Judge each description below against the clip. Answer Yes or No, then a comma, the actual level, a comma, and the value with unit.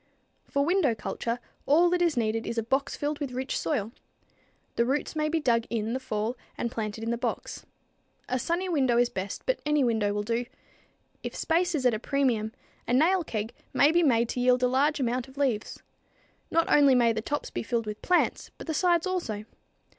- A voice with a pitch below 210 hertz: No, very high, 255 Hz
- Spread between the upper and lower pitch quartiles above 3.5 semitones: Yes, average, 4.7 semitones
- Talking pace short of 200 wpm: No, fast, 205 wpm